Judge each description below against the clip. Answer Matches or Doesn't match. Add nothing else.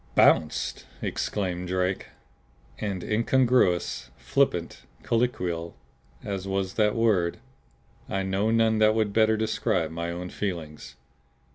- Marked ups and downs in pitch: Doesn't match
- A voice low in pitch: Matches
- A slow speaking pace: Matches